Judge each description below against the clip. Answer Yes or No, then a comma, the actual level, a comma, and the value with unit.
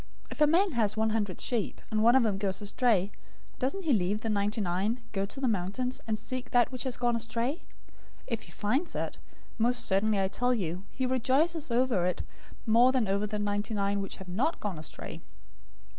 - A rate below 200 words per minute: No, fast, 205 wpm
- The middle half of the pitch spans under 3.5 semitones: No, average, 4.0 semitones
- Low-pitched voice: No, high, 220 Hz